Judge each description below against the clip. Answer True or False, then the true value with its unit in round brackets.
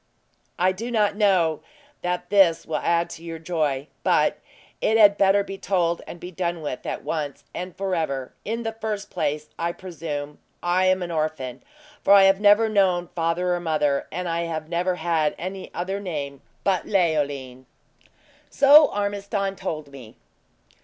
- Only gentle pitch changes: False (3.8 semitones)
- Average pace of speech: True (165 wpm)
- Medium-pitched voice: True (175 Hz)